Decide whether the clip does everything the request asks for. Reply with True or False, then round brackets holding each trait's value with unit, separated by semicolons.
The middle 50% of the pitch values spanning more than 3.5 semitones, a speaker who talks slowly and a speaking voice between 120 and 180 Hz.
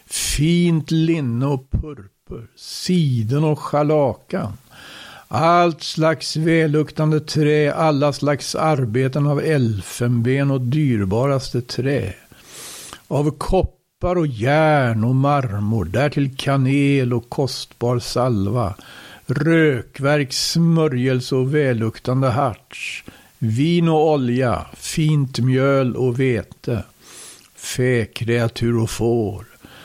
True (3.9 semitones; 90 wpm; 135 Hz)